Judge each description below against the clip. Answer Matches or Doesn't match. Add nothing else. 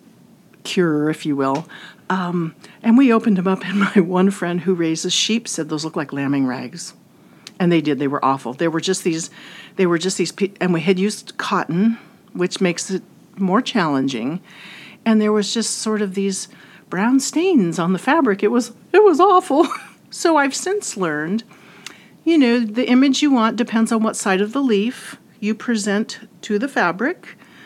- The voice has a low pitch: Doesn't match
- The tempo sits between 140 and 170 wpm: Doesn't match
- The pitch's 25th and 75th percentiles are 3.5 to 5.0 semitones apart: Matches